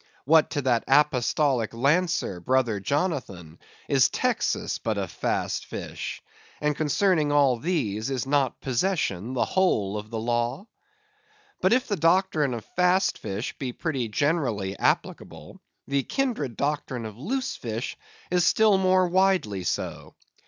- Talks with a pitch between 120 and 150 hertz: Yes, medium, 140 Hz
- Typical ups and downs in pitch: No, wide, 7.3 semitones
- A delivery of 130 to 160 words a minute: Yes, average, 140 wpm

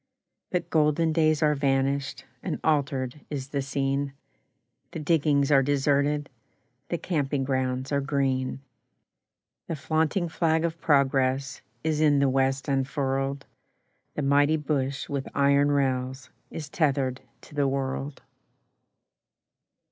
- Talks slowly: Yes, slow, 120 wpm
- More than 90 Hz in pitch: Yes, medium, 140 Hz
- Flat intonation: Yes, narrow, 2.0 semitones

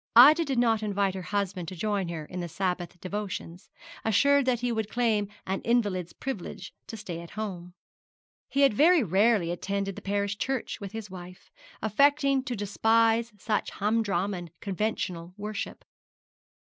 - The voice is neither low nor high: No, high, 205 Hz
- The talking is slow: No, average, 160 wpm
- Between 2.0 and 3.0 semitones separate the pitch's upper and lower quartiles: No, average, 3.8 semitones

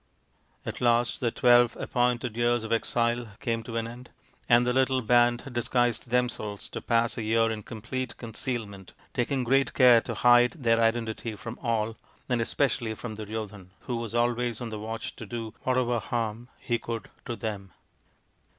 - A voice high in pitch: No, low, 120 Hz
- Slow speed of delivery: No, average, 170 wpm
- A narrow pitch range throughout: Yes, narrow, 1.5 semitones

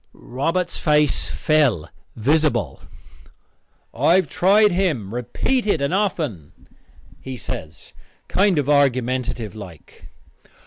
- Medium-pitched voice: Yes, medium, 145 Hz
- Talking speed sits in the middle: No, slow, 95 wpm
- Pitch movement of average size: No, wide, 6.9 semitones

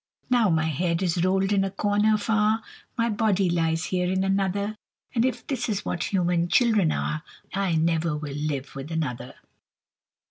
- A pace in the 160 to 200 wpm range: Yes, average, 170 wpm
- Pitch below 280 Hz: Yes, medium, 185 Hz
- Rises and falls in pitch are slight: No, average, 4.2 semitones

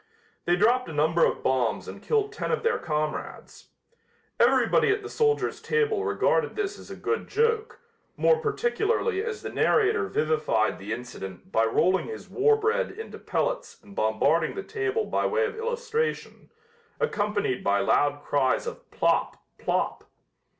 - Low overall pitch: No, very high, 410 Hz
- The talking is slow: No, average, 155 wpm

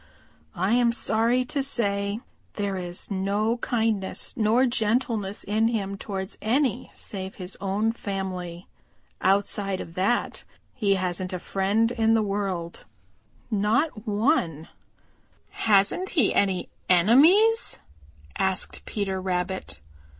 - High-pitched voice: Yes, high, 205 Hz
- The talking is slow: Yes, slow, 115 wpm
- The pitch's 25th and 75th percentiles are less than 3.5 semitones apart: Yes, average, 3.1 semitones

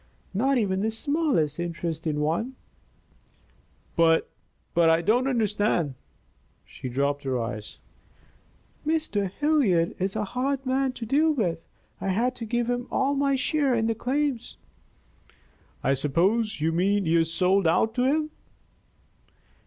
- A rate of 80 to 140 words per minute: Yes, slow, 135 wpm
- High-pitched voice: Yes, high, 215 Hz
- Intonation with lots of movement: Yes, wide, 7.8 semitones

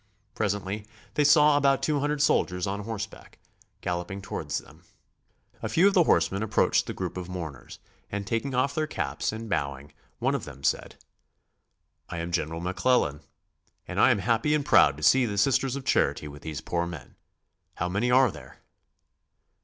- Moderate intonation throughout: No, wide, 7.7 semitones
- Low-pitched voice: Yes, low, 100 Hz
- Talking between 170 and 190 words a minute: Yes, average, 175 wpm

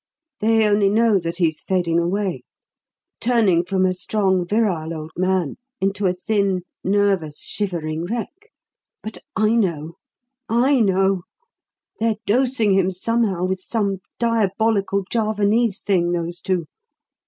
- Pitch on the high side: Yes, high, 195 Hz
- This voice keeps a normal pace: No, slow, 125 wpm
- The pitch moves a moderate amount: Yes, average, 3.5 semitones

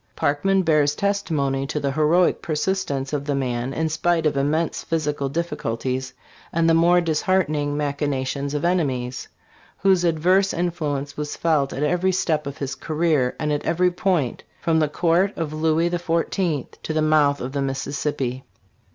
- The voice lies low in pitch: No, medium, 155 Hz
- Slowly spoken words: No, average, 165 wpm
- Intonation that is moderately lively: Yes, average, 3.3 semitones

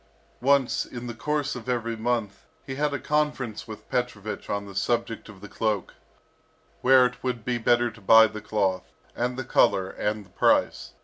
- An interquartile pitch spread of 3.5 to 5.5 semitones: No, average, 3.0 semitones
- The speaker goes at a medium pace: Yes, average, 185 wpm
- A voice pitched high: No, low, 120 Hz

